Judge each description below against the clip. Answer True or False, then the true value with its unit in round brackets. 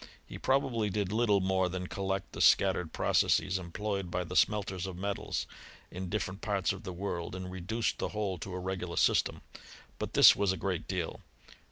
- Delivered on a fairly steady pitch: True (1.9 semitones)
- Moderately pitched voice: False (95 Hz)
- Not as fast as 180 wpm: False (185 wpm)